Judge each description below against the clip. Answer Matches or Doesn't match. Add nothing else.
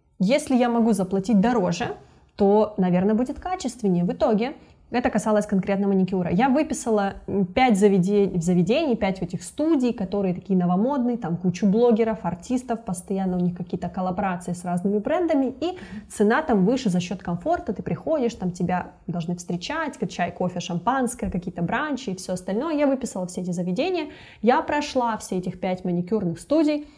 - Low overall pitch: Doesn't match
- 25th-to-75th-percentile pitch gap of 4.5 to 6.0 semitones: Matches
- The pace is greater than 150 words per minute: Matches